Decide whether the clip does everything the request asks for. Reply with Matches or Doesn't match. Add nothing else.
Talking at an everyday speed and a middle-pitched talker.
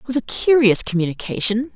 Doesn't match